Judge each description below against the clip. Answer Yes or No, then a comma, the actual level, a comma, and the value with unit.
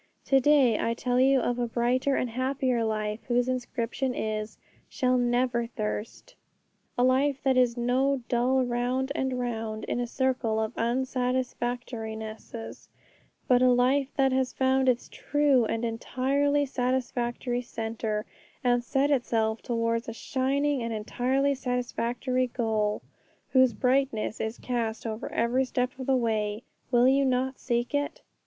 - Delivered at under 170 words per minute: Yes, average, 145 wpm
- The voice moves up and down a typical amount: No, narrow, 2.1 semitones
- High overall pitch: Yes, high, 245 Hz